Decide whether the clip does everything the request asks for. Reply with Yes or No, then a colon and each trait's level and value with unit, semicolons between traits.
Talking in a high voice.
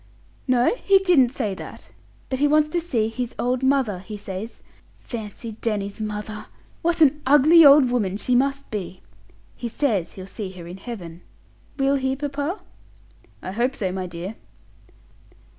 Yes: high, 240 Hz